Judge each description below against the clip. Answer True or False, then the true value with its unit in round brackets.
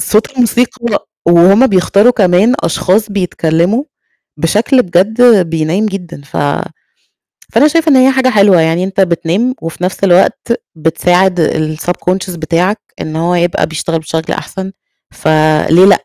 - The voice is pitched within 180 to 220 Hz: True (185 Hz)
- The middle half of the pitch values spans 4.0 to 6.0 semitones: True (4.5 semitones)